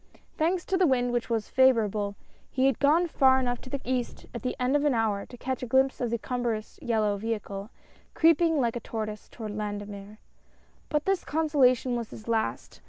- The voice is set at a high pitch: Yes, high, 245 Hz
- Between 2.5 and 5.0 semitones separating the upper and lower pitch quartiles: Yes, average, 3.7 semitones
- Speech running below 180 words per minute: No, average, 195 wpm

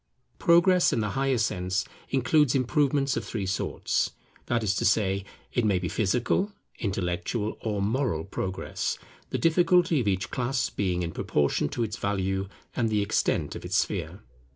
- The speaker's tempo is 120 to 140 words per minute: No, average, 160 wpm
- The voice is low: Yes, low, 110 Hz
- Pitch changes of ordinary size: No, wide, 5.7 semitones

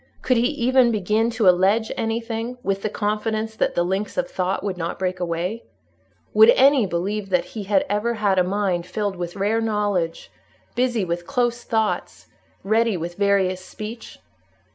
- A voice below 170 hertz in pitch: No, high, 210 Hz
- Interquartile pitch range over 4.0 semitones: No, average, 3.7 semitones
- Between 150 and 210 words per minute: Yes, average, 165 wpm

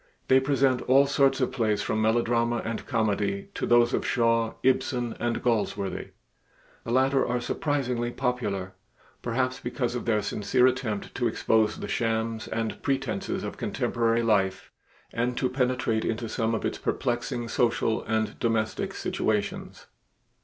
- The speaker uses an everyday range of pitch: No, narrow, 2.3 semitones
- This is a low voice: Yes, low, 115 Hz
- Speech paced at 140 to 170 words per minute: Yes, average, 145 wpm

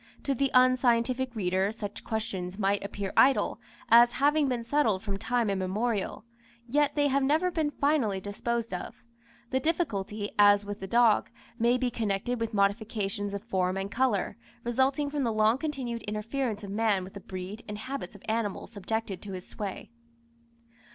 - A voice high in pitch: Yes, high, 225 Hz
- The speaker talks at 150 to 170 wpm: Yes, average, 165 wpm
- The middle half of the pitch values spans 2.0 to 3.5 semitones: No, average, 4.1 semitones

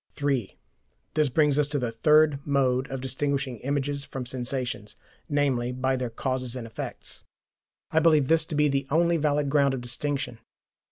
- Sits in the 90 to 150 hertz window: Yes, medium, 140 Hz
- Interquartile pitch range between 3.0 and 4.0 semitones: No, narrow, 2.5 semitones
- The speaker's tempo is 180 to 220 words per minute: No, average, 165 wpm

